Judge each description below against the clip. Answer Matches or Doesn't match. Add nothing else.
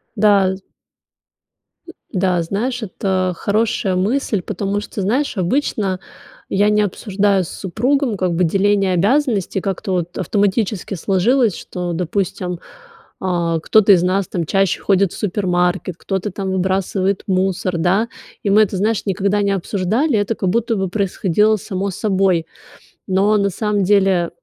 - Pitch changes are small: Matches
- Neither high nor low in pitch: Doesn't match